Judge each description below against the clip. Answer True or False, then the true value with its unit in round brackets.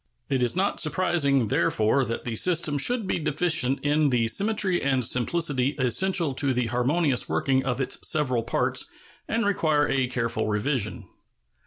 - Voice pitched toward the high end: False (140 Hz)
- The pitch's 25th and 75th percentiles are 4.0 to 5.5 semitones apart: True (4.9 semitones)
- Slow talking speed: False (155 wpm)